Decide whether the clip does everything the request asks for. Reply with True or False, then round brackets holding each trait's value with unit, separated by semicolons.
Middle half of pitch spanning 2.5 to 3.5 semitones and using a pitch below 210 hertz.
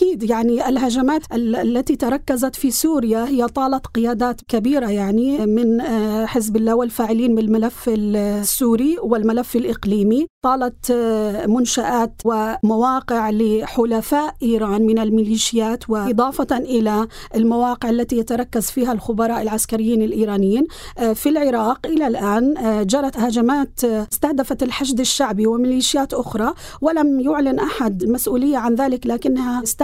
False (2.9 semitones; 235 Hz)